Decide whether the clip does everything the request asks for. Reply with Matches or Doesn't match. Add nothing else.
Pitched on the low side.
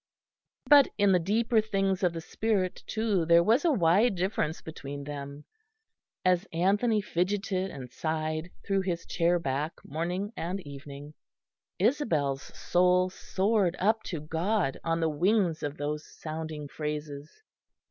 Doesn't match